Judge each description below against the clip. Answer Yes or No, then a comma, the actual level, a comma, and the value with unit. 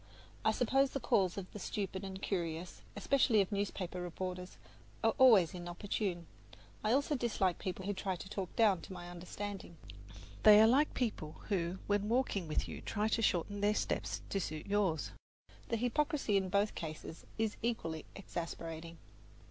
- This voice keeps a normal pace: Yes, average, 165 wpm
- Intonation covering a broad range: No, average, 3.5 semitones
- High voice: Yes, high, 195 Hz